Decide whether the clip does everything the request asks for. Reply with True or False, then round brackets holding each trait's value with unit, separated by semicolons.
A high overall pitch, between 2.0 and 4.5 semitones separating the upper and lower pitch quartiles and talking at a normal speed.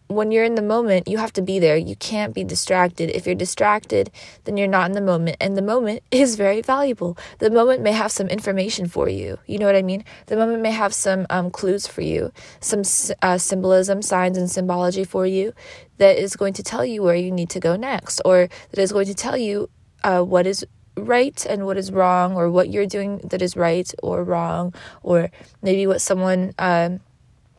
False (195 Hz; 2.5 semitones; 215 wpm)